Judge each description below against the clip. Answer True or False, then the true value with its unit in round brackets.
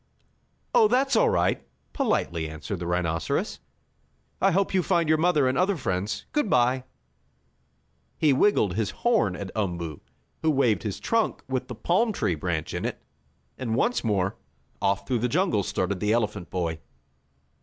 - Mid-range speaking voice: False (120 Hz)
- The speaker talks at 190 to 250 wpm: False (160 wpm)